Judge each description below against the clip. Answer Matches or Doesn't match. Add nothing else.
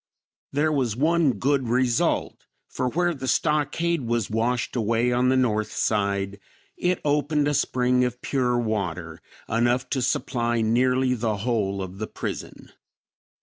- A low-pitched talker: Matches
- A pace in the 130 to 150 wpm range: Matches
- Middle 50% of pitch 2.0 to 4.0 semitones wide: Matches